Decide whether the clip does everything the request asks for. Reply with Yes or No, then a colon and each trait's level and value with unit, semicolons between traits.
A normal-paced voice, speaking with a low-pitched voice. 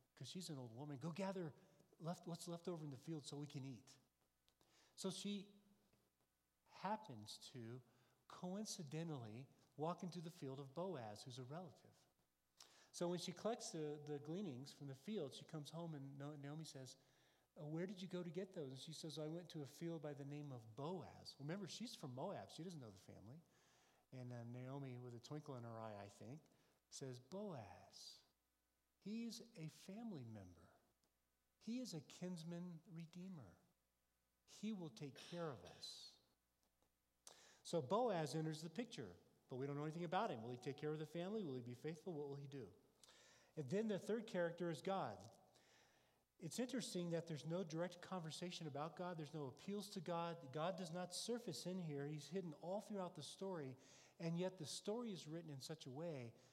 No: average, 185 wpm; medium, 155 Hz